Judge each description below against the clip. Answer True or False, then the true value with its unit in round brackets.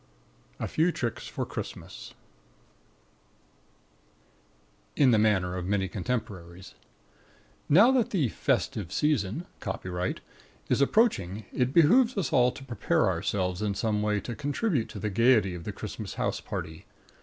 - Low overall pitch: True (110 Hz)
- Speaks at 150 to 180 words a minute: False (135 wpm)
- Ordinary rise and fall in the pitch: False (7.4 semitones)